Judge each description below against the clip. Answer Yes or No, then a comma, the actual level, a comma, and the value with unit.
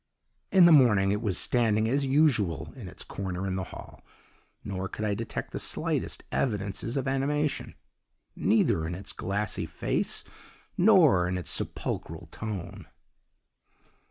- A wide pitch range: Yes, wide, 6.0 semitones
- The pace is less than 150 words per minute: Yes, average, 140 wpm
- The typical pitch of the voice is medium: No, low, 105 Hz